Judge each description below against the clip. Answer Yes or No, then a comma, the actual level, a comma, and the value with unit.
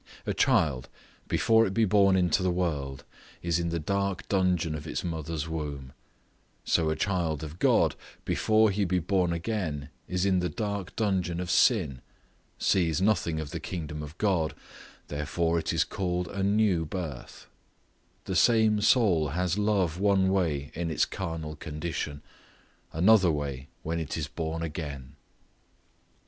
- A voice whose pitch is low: Yes, very low, 85 Hz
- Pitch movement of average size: Yes, average, 3.7 semitones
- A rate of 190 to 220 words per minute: No, average, 155 wpm